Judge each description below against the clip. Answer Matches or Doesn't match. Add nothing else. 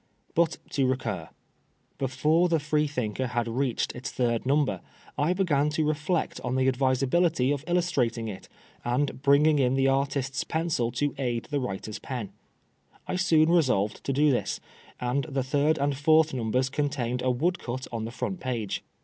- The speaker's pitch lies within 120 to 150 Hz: Matches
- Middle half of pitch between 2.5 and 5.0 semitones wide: Matches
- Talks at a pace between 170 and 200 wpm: Doesn't match